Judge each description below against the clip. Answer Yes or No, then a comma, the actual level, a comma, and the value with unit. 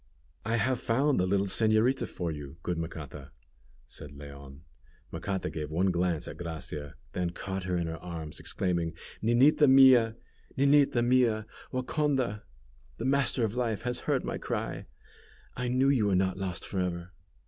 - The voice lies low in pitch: Yes, very low, 95 Hz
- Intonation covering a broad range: Yes, wide, 6.6 semitones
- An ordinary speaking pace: Yes, average, 160 wpm